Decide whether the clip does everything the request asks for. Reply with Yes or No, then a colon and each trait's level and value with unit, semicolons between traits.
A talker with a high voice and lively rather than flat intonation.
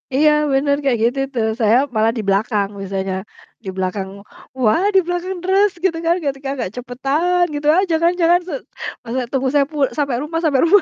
Yes: very high, 275 Hz; wide, 6.6 semitones